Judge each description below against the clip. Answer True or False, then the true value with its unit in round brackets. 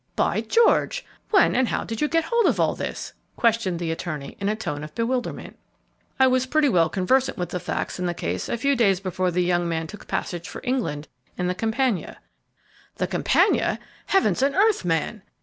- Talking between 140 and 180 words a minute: False (200 wpm)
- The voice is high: True (210 Hz)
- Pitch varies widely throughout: True (7.0 semitones)